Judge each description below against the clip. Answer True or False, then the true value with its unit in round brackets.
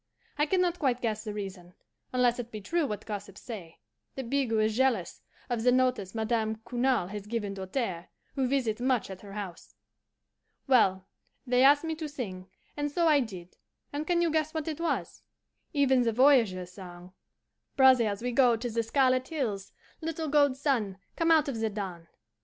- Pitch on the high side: True (240 Hz)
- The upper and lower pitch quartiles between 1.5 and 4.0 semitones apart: False (5.4 semitones)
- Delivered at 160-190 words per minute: True (180 wpm)